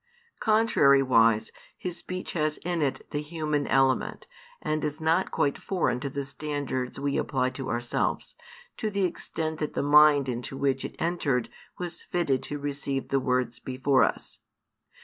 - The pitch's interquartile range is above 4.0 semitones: No, average, 3.1 semitones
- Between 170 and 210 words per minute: No, average, 160 wpm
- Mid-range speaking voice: Yes, medium, 145 Hz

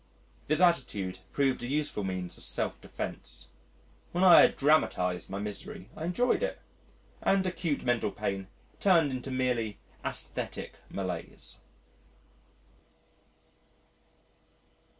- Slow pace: Yes, slow, 110 wpm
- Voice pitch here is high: No, low, 130 Hz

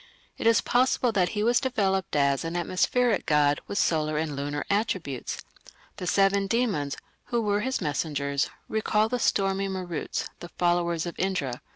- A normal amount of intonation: No, wide, 5.7 semitones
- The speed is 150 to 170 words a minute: Yes, average, 160 wpm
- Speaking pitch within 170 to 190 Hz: Yes, medium, 185 Hz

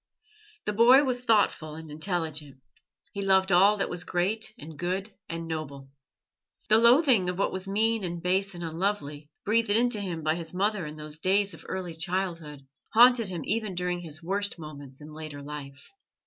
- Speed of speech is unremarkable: Yes, average, 175 wpm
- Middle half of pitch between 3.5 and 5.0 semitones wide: Yes, average, 4.6 semitones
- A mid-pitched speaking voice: Yes, medium, 180 Hz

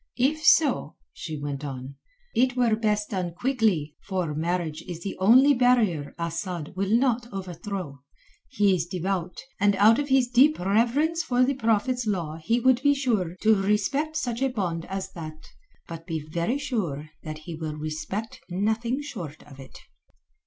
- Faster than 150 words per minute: Yes, average, 165 wpm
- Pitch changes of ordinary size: No, wide, 6.9 semitones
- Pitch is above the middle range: Yes, high, 195 Hz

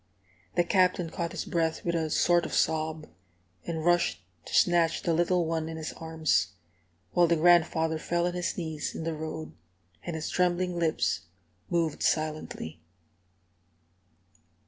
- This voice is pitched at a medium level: Yes, medium, 165 Hz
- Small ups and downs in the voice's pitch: Yes, narrow, 1.6 semitones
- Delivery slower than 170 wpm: Yes, average, 145 wpm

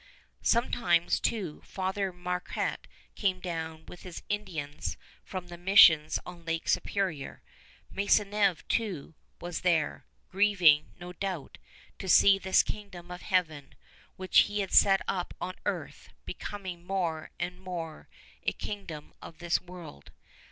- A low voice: No, medium, 180 Hz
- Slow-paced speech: Yes, slow, 130 wpm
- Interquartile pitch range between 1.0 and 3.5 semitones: Yes, average, 2.8 semitones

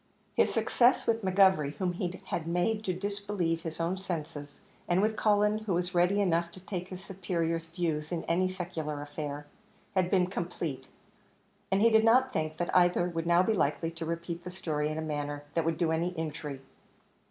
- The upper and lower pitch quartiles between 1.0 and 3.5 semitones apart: Yes, average, 2.8 semitones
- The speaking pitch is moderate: Yes, medium, 175 Hz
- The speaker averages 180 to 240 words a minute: Yes, average, 190 wpm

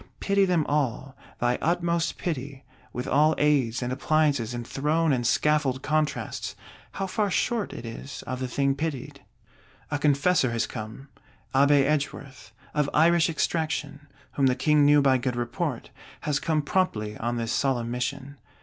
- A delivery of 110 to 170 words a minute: Yes, average, 155 wpm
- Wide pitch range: No, average, 3.4 semitones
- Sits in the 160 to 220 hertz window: No, medium, 140 Hz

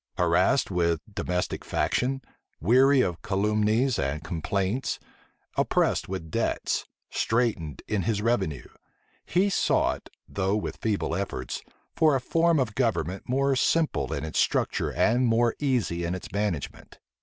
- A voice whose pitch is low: Yes, low, 105 Hz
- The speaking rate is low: Yes, slow, 130 wpm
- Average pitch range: No, wide, 6.3 semitones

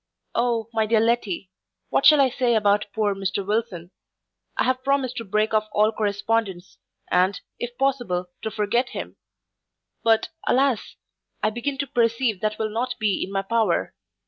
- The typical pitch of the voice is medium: No, high, 220 Hz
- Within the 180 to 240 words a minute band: No, average, 165 wpm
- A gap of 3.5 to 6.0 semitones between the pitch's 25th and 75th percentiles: No, average, 2.9 semitones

